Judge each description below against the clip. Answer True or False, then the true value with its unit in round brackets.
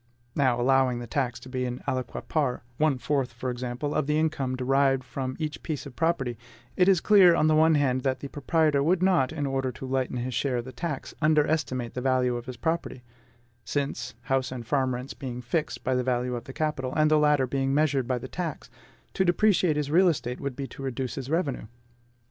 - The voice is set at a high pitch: False (135 Hz)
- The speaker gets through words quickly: True (220 wpm)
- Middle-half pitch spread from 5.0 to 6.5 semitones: False (3.2 semitones)